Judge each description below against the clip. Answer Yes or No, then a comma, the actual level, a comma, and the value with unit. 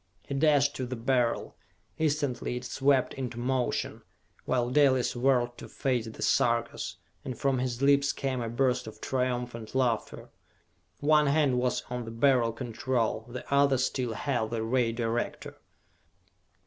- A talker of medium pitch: No, low, 125 Hz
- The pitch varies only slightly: Yes, narrow, 2.2 semitones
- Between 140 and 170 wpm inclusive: Yes, average, 150 wpm